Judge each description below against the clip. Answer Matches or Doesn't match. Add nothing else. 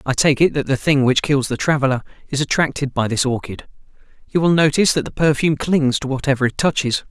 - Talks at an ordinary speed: Doesn't match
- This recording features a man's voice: Matches